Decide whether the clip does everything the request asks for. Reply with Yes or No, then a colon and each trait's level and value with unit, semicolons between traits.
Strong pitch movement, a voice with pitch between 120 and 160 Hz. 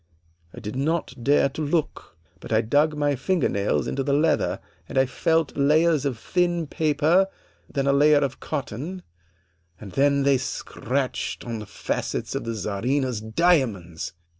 No: average, 4.4 semitones; medium, 140 Hz